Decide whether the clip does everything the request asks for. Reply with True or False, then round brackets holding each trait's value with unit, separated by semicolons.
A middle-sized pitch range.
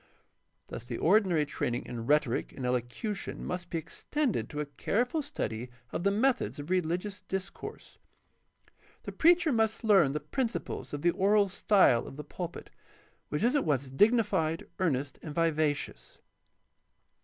False (6.5 semitones)